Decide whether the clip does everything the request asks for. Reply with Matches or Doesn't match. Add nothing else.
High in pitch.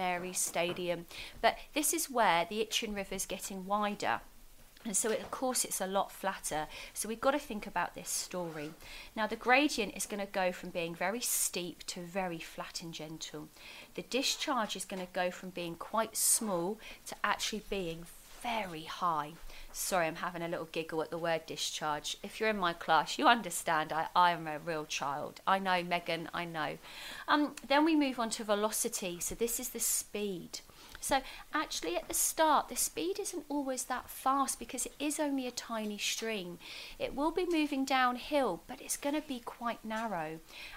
Matches